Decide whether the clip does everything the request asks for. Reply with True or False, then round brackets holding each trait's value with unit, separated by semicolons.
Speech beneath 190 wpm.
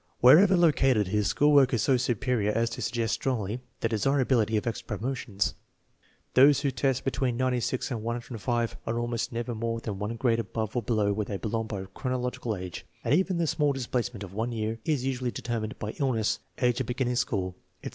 False (200 wpm)